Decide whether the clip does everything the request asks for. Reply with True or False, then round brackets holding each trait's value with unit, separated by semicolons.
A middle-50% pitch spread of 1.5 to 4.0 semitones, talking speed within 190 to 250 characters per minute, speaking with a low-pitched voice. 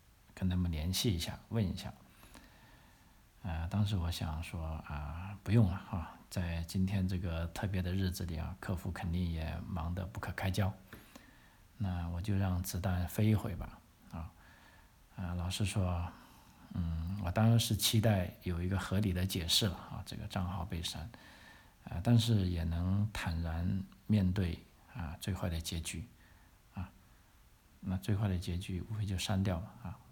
True (2.5 semitones; 225 characters per minute; 95 Hz)